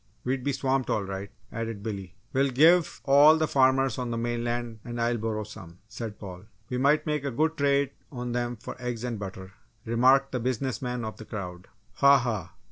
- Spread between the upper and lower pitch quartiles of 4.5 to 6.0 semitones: No, average, 3.6 semitones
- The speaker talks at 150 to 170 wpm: No, average, 195 wpm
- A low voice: Yes, low, 120 Hz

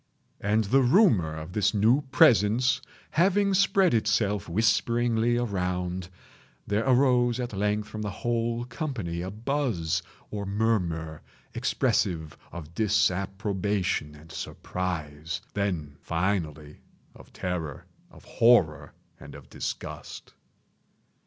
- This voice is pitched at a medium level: No, low, 105 Hz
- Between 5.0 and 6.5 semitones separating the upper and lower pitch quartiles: Yes, wide, 5.5 semitones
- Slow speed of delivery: Yes, slow, 105 wpm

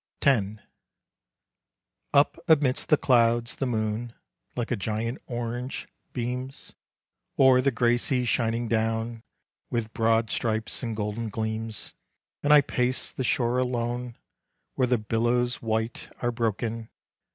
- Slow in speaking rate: Yes, slow, 125 wpm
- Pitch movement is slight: Yes, narrow, 1.9 semitones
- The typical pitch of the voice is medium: No, low, 120 Hz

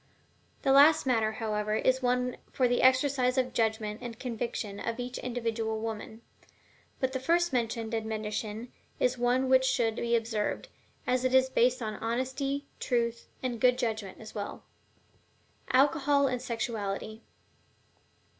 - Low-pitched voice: No, high, 240 Hz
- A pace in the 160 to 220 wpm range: No, average, 145 wpm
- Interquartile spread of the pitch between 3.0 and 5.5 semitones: No, narrow, 2.6 semitones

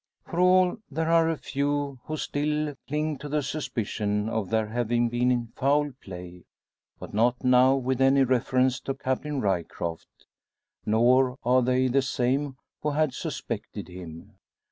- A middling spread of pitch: Yes, average, 4.1 semitones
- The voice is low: Yes, low, 130 Hz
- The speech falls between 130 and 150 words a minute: Yes, average, 145 wpm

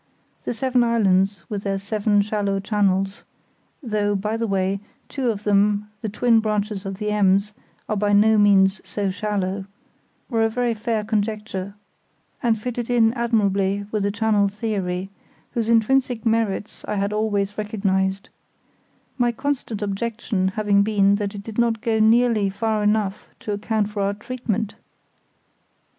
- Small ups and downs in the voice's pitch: Yes, narrow, 2.1 semitones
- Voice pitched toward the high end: Yes, high, 210 Hz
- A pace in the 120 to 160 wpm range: Yes, average, 150 wpm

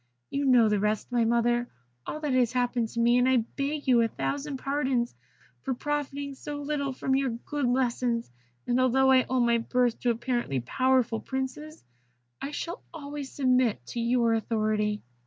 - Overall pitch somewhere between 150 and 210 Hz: No, very high, 250 Hz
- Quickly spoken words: No, average, 175 wpm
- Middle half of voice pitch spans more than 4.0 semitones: No, average, 2.8 semitones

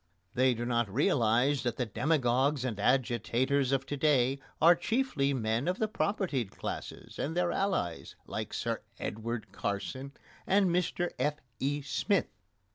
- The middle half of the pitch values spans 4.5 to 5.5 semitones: Yes, average, 5.1 semitones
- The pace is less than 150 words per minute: Yes, average, 140 wpm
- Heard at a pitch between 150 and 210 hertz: No, low, 135 Hz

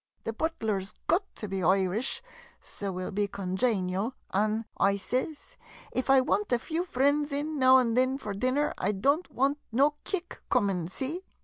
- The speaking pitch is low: No, high, 245 Hz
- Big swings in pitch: Yes, wide, 6.2 semitones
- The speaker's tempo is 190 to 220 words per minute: Yes, average, 195 wpm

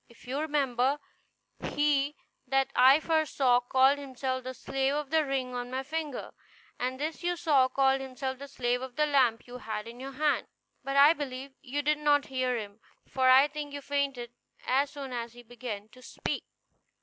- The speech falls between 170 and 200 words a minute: Yes, average, 190 wpm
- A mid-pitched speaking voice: No, very high, 270 Hz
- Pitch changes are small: Yes, narrow, 2.3 semitones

